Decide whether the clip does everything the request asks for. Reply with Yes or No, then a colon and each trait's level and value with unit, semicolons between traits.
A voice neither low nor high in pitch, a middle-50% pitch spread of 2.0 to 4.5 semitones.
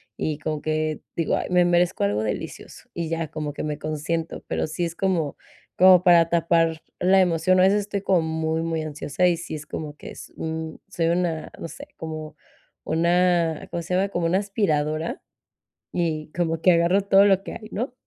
Yes: medium, 165 Hz; narrow, 2.5 semitones